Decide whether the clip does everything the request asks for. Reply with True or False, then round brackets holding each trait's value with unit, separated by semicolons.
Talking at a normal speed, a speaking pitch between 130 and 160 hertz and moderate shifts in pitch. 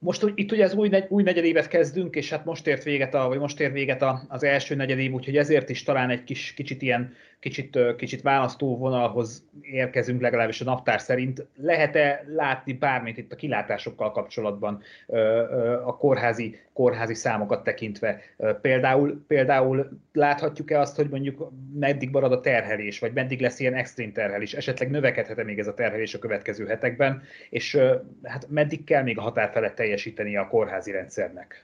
False (170 wpm; 135 Hz; 3.1 semitones)